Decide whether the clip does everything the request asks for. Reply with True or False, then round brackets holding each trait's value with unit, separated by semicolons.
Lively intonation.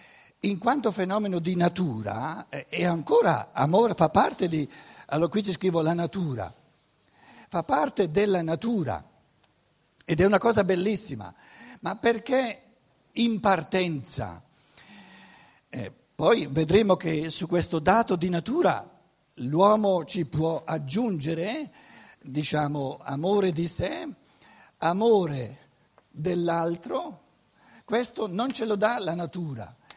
False (4.7 semitones)